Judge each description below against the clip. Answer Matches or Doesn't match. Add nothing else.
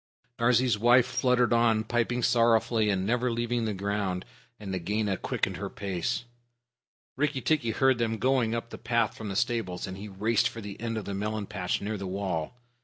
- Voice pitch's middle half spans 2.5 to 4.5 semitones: Matches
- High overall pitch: Doesn't match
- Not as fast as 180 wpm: Doesn't match